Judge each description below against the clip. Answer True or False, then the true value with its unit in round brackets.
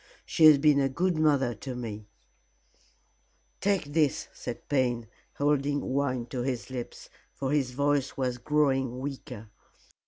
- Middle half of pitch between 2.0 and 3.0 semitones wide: True (2.6 semitones)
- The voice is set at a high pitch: False (135 Hz)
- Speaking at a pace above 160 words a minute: False (145 wpm)